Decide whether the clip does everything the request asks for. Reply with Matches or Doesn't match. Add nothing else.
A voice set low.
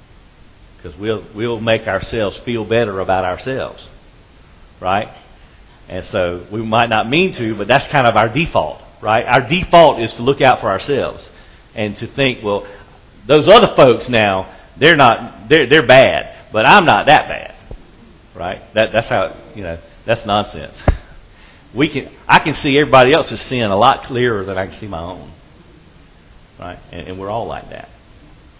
Matches